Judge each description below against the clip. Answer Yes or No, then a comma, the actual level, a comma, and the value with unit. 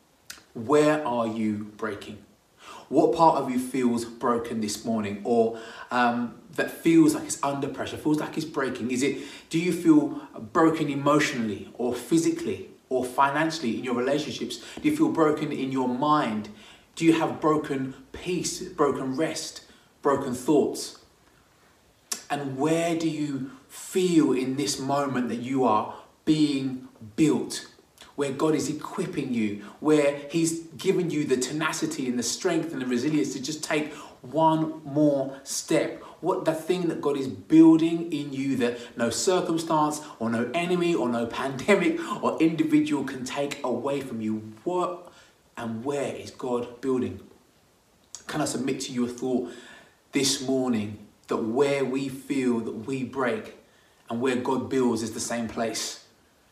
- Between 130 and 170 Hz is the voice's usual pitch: Yes, low, 135 Hz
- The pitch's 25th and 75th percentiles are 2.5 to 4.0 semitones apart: No, average, 4.5 semitones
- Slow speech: No, average, 155 wpm